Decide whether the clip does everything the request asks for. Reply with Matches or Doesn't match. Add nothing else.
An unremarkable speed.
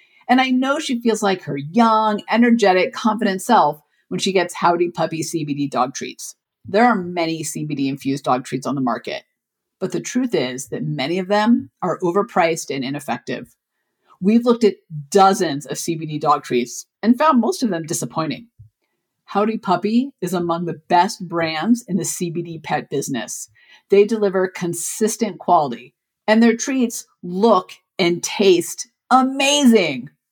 Matches